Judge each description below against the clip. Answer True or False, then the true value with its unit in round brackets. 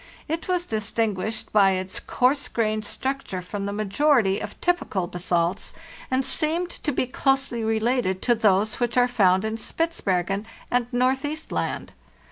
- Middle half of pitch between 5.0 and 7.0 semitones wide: True (5.3 semitones)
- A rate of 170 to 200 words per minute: False (145 wpm)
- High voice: True (225 Hz)